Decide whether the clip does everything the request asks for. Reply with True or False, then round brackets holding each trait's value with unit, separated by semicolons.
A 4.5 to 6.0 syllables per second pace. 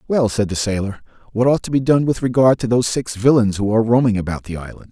False (6.5 syllables/s)